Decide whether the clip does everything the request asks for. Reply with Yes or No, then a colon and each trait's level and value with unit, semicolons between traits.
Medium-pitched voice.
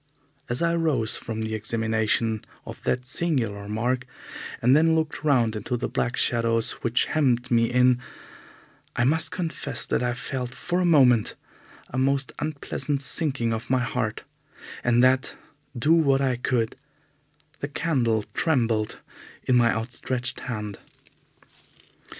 No: low, 125 Hz